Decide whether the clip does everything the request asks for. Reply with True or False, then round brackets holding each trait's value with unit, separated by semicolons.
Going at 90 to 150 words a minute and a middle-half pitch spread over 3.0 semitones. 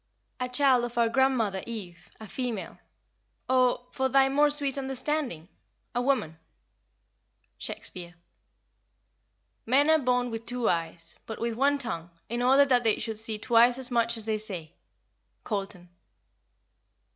True (140 wpm; 3.7 semitones)